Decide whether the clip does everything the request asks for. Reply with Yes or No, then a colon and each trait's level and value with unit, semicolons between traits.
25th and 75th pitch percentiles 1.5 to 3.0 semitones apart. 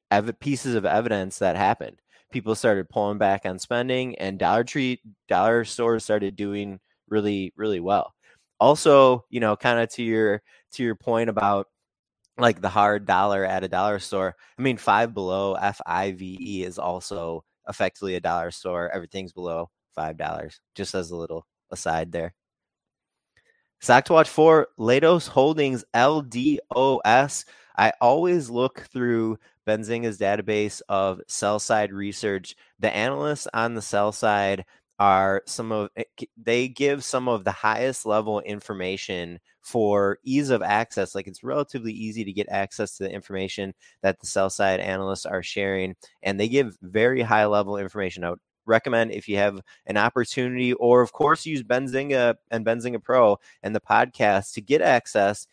No: average, 3.9 semitones